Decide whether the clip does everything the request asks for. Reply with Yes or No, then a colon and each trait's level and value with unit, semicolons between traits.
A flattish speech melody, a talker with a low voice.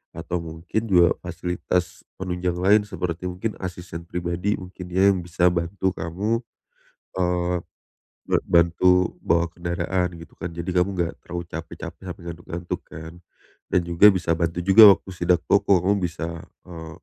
Yes: narrow, 1.4 semitones; very low, 90 Hz